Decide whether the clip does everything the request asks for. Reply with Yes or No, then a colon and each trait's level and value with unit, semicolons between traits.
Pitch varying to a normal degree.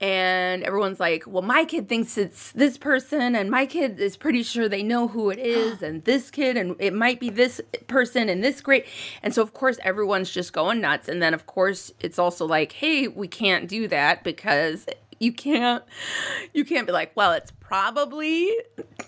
No: wide, 5.8 semitones